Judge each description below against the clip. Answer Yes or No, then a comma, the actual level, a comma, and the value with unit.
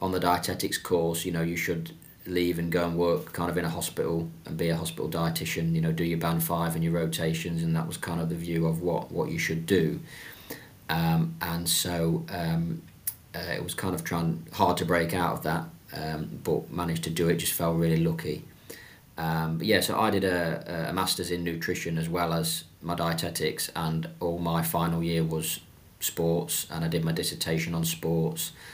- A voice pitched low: Yes, very low, 85 Hz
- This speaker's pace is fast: Yes, fast, 210 wpm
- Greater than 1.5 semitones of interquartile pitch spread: No, narrow, 0.8 semitones